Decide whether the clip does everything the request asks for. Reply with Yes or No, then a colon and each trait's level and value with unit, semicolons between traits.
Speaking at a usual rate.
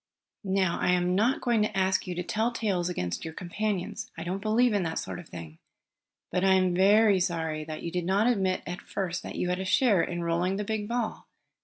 No: fast, 225 wpm